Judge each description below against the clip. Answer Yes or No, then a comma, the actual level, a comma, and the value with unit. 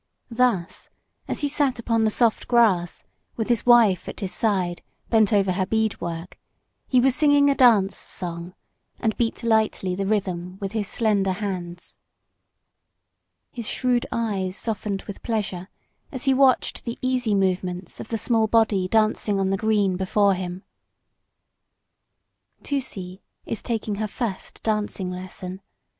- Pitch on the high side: Yes, high, 210 Hz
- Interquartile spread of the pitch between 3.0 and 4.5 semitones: Yes, average, 3.7 semitones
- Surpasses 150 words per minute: No, average, 145 wpm